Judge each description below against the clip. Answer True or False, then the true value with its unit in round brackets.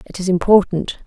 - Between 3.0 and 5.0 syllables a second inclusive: False (5.6 syllables/s)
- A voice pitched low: False (185 Hz)